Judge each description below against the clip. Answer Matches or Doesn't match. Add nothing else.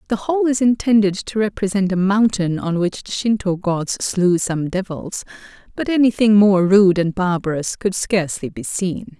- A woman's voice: Matches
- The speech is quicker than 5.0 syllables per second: Doesn't match